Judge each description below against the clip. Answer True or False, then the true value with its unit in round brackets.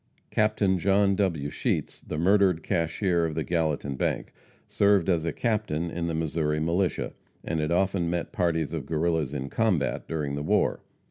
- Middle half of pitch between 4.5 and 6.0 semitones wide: False (3.7 semitones)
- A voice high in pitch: False (85 Hz)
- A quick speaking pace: False (165 wpm)